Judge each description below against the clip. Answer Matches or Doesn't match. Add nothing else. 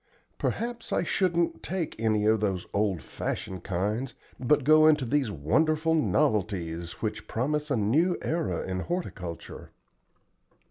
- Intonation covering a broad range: Matches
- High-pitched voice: Doesn't match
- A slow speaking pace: Matches